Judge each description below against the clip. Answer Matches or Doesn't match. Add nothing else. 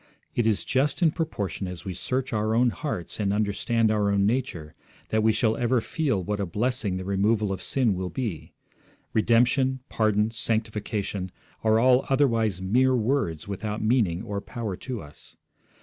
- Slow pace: Doesn't match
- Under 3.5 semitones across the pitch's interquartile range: Doesn't match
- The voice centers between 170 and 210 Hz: Doesn't match